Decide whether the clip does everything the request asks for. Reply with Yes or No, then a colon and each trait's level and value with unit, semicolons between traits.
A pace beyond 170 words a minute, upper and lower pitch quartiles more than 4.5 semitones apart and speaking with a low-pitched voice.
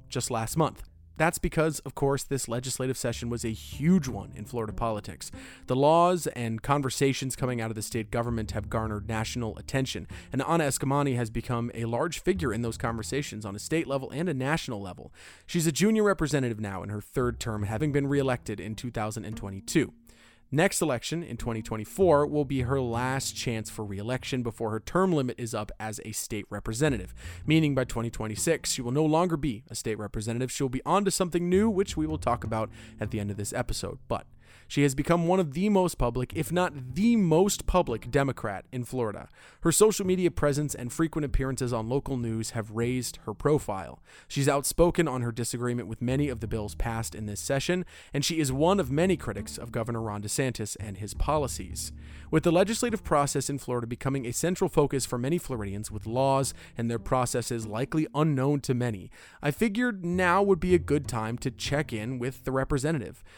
Yes: average, 200 wpm; average, 5.2 semitones; low, 125 Hz